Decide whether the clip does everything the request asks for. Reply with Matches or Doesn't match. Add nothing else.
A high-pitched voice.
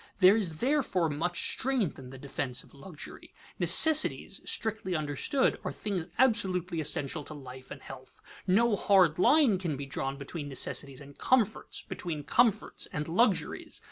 Doesn't match